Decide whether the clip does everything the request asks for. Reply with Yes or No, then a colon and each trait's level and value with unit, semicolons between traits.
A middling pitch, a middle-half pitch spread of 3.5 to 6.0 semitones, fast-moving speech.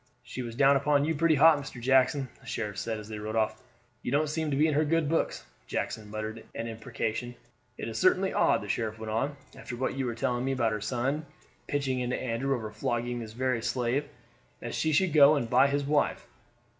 No: low, 125 Hz; average, 4.0 semitones; fast, 220 wpm